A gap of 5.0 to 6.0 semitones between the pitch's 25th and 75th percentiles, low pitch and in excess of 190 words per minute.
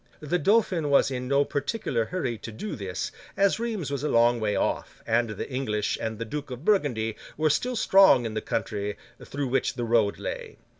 Yes: wide, 5.6 semitones; low, 130 Hz; average, 200 wpm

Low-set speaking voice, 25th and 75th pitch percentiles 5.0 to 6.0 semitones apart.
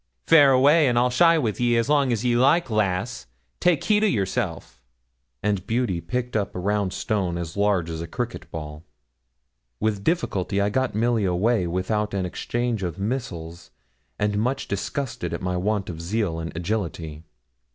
Yes: low, 105 Hz; average, 5.3 semitones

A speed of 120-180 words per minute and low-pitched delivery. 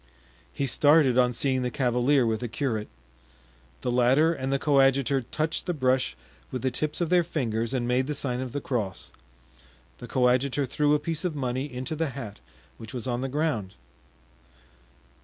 Yes: average, 175 wpm; low, 130 Hz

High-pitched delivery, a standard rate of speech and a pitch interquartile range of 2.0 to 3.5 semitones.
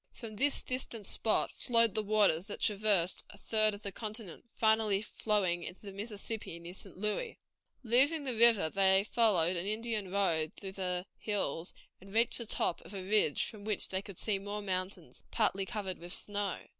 Yes: high, 205 Hz; average, 180 wpm; narrow, 2.5 semitones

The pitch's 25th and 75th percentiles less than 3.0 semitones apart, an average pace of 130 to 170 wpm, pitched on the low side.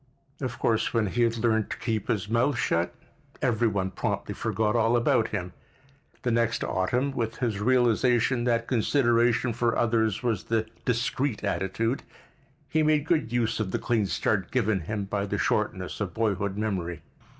Yes: narrow, 2.6 semitones; average, 165 wpm; low, 115 Hz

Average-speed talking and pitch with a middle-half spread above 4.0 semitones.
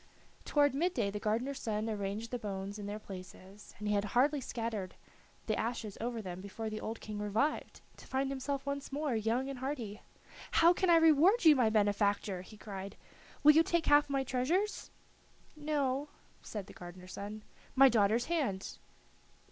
Yes: average, 175 wpm; wide, 5.4 semitones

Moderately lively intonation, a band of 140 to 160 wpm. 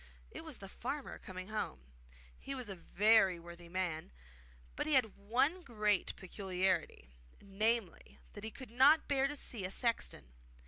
Yes: average, 4.8 semitones; average, 155 wpm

